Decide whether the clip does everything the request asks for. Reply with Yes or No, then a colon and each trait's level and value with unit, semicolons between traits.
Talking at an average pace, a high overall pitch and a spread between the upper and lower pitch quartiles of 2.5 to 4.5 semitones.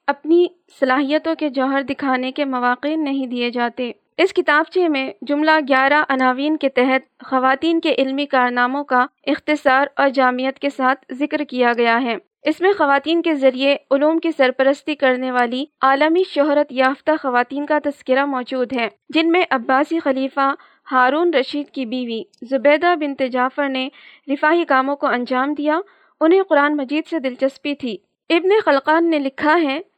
Yes: average, 155 wpm; very high, 280 Hz; average, 2.8 semitones